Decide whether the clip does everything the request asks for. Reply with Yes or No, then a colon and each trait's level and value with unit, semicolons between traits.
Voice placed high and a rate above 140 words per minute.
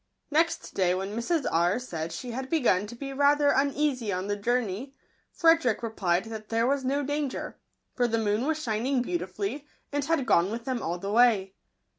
Yes: high, 240 Hz; average, 185 wpm